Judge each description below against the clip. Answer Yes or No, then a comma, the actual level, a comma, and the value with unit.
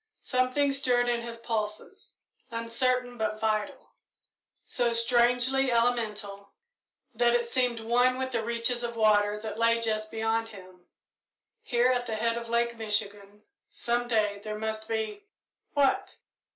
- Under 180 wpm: Yes, average, 140 wpm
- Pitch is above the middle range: Yes, high, 230 Hz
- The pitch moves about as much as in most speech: No, narrow, 2.0 semitones